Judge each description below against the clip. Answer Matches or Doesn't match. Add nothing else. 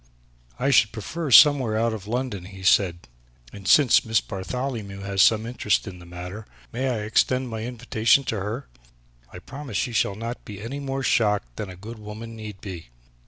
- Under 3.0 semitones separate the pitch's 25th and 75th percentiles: Doesn't match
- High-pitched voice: Doesn't match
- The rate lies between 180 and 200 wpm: Matches